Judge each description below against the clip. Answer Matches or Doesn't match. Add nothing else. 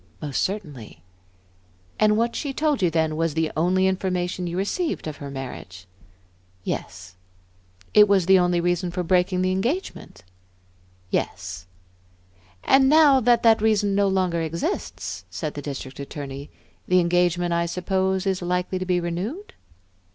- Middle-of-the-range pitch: Matches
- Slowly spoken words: Doesn't match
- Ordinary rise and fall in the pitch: Matches